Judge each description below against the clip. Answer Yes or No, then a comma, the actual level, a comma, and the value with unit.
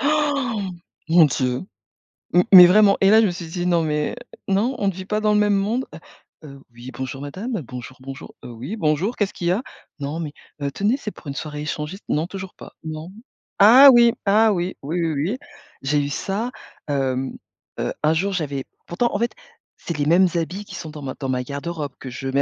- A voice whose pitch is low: No, medium, 170 Hz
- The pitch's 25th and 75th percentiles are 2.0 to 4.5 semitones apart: No, wide, 6.2 semitones